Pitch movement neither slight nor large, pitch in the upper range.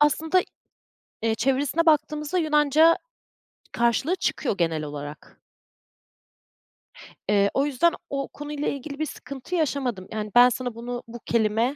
Yes: average, 4.9 semitones; very high, 270 Hz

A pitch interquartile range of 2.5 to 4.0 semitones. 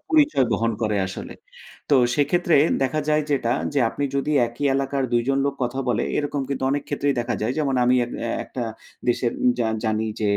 Yes: average, 3.3 semitones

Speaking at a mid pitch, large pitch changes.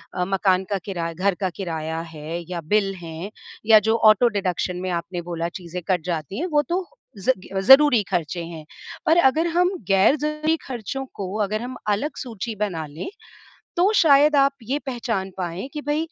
No: high, 200 Hz; wide, 7.4 semitones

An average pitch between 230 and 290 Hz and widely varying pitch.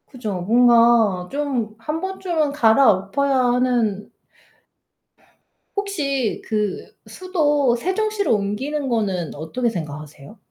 Yes: high, 240 Hz; wide, 5.9 semitones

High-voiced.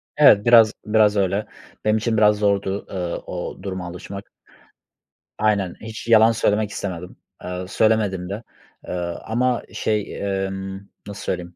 No: low, 105 Hz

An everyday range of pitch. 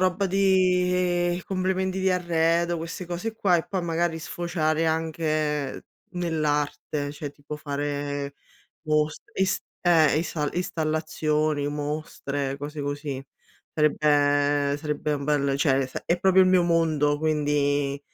Yes: average, 3.1 semitones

